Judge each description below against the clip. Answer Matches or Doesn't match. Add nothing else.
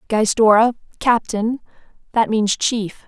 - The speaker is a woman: Matches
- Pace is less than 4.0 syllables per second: Matches